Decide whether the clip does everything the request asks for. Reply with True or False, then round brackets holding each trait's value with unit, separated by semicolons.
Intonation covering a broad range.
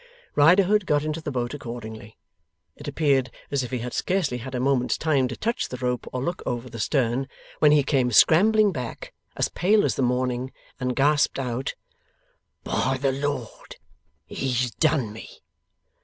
False (3.4 semitones)